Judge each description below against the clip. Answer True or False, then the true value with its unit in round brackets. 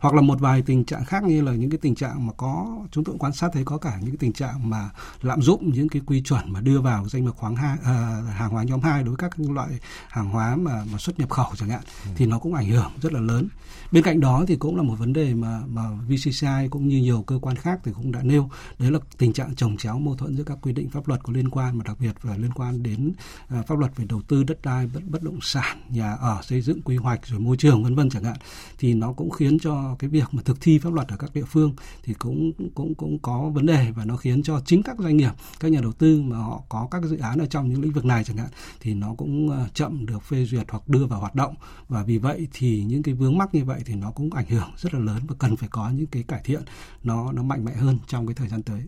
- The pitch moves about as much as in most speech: True (4.0 semitones)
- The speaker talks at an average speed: False (285 wpm)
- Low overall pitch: True (130 Hz)